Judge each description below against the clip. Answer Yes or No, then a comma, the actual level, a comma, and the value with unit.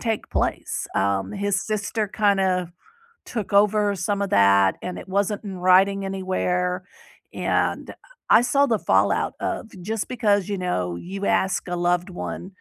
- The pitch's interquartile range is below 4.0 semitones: Yes, narrow, 2.4 semitones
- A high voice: Yes, high, 195 Hz